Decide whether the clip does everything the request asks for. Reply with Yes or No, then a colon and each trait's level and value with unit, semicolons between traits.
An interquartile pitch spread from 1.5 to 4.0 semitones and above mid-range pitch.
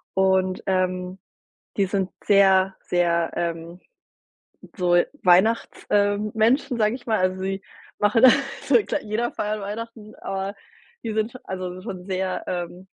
Yes: narrow, 2.6 semitones; high, 195 Hz